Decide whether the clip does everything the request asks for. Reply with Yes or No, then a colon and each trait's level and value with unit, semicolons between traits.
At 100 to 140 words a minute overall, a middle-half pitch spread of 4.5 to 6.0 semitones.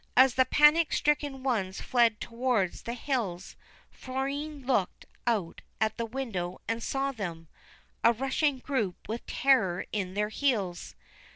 Yes: slow, 135 wpm; average, 5.0 semitones